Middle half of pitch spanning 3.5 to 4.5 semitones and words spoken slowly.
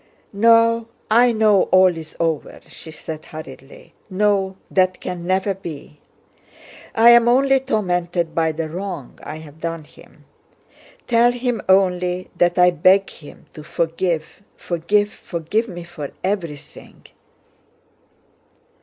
Yes: average, 4.1 semitones; slow, 120 wpm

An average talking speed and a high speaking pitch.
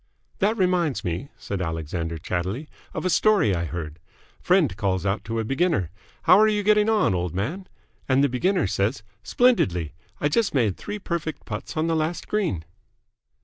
No: average, 175 wpm; low, 130 Hz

